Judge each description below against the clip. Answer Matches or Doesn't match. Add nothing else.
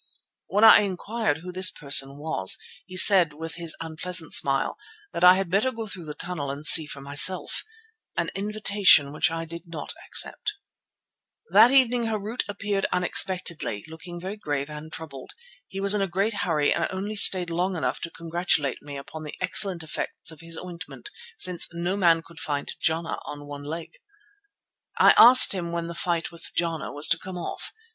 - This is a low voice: Doesn't match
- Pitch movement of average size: Matches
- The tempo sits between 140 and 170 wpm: Doesn't match